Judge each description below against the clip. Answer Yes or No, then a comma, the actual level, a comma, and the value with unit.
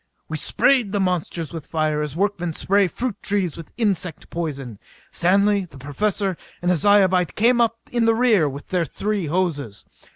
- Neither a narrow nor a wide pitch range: Yes, average, 4.4 semitones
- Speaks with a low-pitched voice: No, medium, 185 Hz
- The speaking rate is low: No, average, 170 wpm